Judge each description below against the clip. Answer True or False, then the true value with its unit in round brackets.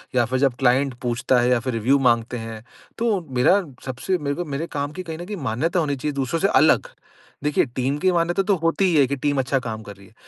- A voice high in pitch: False (140 Hz)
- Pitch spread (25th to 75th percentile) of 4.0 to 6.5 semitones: True (5.1 semitones)